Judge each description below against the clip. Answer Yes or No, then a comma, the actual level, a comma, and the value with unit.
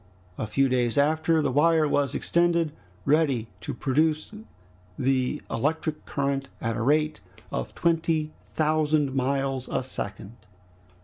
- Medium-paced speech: No, slow, 125 wpm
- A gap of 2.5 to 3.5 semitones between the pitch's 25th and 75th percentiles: Yes, average, 3.1 semitones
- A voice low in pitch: No, medium, 145 Hz